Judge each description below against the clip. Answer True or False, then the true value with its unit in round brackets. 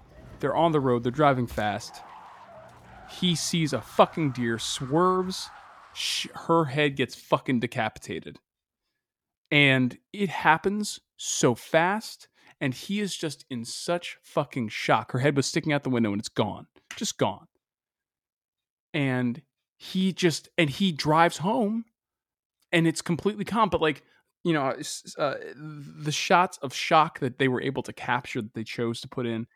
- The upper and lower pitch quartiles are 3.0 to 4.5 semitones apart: False (5.4 semitones)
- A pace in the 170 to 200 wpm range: False (155 wpm)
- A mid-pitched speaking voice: True (150 Hz)